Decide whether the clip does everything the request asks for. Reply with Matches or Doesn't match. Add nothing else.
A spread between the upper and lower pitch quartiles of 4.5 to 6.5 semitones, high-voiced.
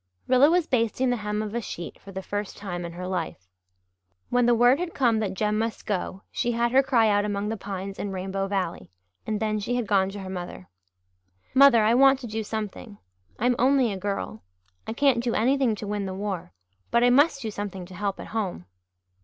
Doesn't match